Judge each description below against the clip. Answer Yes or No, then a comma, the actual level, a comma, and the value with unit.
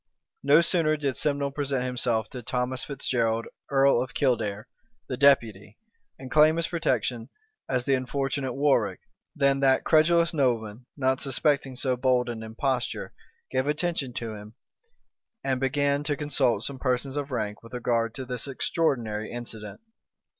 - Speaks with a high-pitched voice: No, low, 130 Hz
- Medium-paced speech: Yes, average, 145 wpm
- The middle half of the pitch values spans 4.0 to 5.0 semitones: No, average, 3.0 semitones